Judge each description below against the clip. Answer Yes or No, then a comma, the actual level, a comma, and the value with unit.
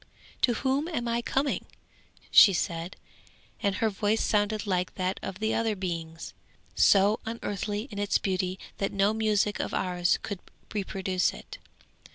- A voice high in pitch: Yes, high, 205 Hz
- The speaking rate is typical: Yes, average, 150 wpm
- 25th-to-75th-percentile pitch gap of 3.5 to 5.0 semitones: No, average, 2.8 semitones